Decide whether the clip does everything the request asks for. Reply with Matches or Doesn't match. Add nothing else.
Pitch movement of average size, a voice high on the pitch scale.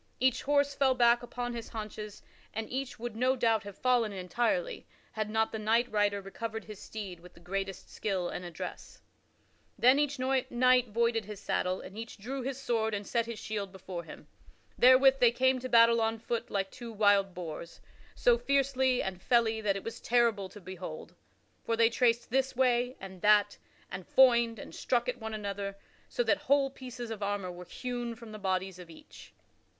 Matches